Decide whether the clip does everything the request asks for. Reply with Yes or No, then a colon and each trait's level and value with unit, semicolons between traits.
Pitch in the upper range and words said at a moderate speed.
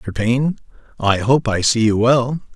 No: low, 120 Hz; average, 190 wpm